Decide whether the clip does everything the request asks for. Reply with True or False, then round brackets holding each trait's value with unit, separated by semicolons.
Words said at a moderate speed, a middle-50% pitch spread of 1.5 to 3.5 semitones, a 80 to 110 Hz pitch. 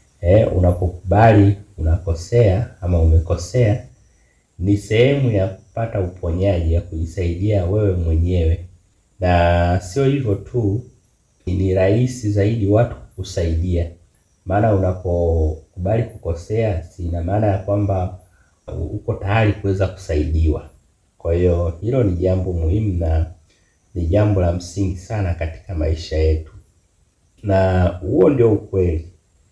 True (110 wpm; 3.2 semitones; 95 Hz)